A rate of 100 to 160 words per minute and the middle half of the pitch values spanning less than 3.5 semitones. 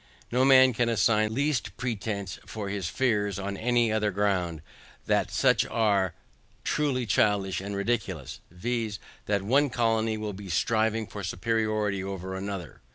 Yes: average, 155 wpm; average, 2.9 semitones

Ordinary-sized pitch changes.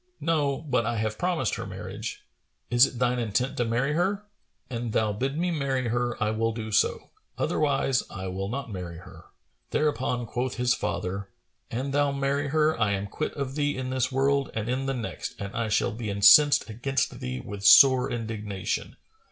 Yes: average, 4.2 semitones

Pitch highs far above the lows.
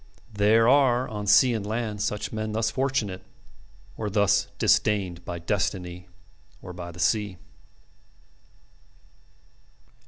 No: average, 3.3 semitones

